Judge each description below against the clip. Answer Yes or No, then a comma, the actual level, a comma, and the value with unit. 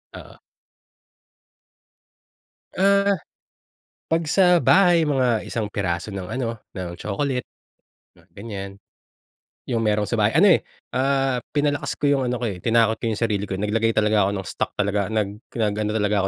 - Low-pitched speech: Yes, low, 115 Hz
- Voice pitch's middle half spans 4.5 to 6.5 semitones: Yes, average, 5.1 semitones